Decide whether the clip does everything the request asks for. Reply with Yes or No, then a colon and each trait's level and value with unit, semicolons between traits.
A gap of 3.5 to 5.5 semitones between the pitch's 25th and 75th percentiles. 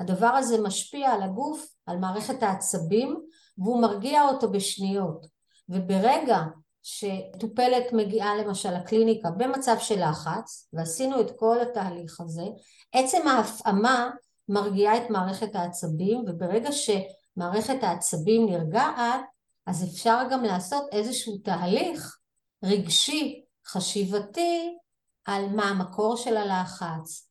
Yes: average, 4.3 semitones